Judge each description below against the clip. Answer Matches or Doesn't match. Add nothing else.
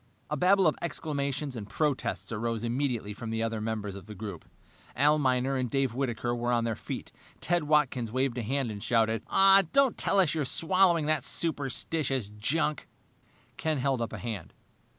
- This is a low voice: Matches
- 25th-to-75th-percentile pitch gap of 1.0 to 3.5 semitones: Doesn't match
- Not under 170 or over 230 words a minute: Matches